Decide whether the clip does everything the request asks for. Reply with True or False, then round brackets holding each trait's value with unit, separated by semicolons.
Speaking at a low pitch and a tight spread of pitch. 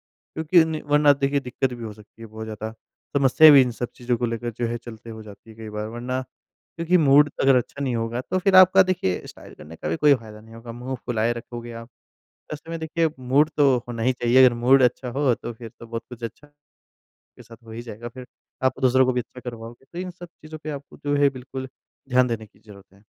False (125 Hz; 3.9 semitones)